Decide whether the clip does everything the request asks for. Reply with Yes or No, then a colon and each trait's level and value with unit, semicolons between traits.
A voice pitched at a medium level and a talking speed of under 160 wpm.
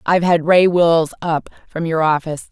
No: medium, 165 Hz; average, 190 wpm